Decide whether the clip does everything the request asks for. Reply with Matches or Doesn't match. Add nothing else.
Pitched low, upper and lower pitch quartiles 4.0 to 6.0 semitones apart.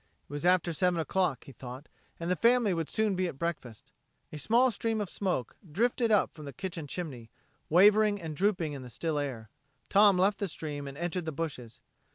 Doesn't match